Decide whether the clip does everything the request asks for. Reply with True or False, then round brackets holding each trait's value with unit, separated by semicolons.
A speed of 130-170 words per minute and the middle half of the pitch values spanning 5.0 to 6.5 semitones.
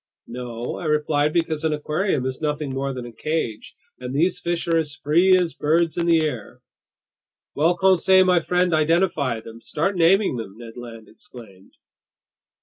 True (165 wpm; 5.4 semitones)